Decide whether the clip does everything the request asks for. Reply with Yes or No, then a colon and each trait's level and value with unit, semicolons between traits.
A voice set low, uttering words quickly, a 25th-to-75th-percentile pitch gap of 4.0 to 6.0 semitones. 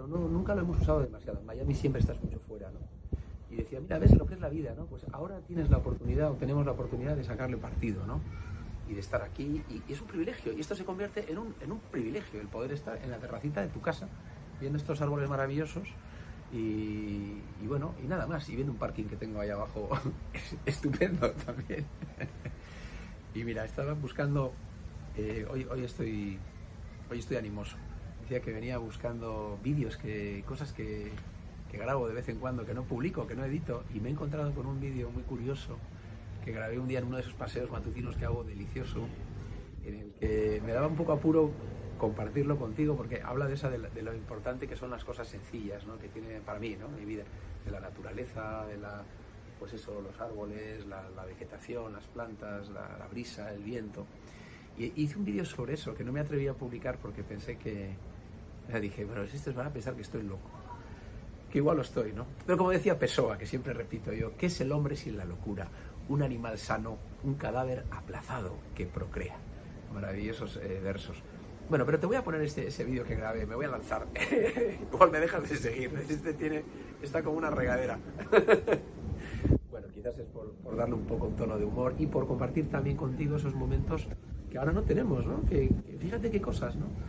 Yes: low, 115 Hz; fast, 205 wpm; average, 4.9 semitones